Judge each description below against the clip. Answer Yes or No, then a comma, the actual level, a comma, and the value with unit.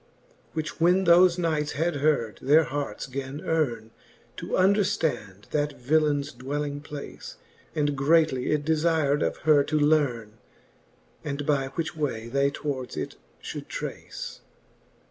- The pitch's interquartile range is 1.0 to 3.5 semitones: Yes, narrow, 2.5 semitones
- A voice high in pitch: No, medium, 145 Hz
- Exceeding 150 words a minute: No, slow, 135 wpm